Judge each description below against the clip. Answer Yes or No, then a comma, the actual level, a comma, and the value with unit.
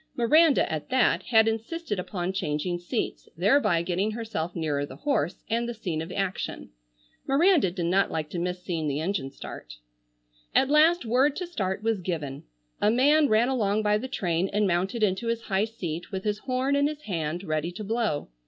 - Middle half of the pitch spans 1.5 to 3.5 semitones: No, wide, 5.6 semitones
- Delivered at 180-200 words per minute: Yes, average, 190 wpm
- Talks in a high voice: Yes, high, 205 Hz